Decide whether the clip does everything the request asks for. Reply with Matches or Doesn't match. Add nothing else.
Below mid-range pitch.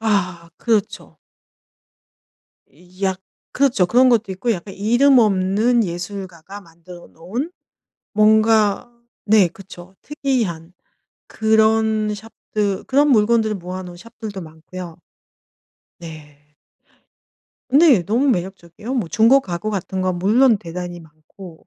Doesn't match